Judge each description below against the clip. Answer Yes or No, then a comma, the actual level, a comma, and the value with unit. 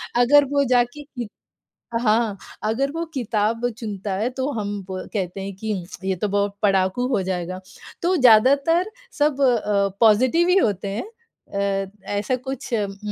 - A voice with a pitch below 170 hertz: No, high, 225 Hz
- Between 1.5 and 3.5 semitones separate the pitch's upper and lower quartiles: No, average, 5.1 semitones